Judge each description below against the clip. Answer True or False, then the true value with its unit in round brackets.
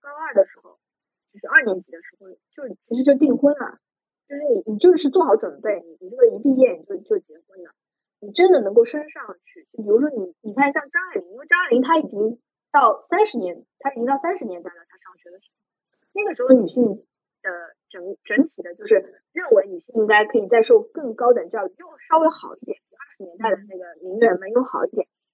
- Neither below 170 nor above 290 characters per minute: False (325 characters per minute)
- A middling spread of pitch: False (8.7 semitones)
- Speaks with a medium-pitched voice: False (275 Hz)